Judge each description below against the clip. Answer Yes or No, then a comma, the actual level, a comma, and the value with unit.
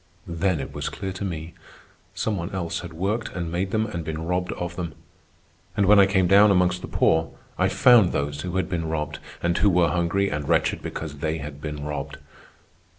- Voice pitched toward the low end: Yes, very low, 85 Hz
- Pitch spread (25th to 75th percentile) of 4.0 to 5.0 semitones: No, average, 3.2 semitones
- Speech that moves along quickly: Yes, fast, 210 wpm